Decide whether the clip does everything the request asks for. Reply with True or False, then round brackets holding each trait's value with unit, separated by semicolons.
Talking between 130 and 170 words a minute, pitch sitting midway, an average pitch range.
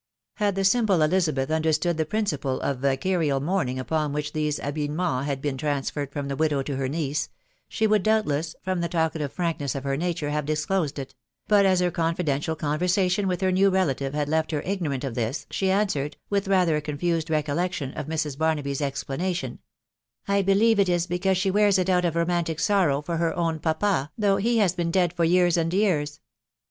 False (200 wpm; 160 Hz; 4.1 semitones)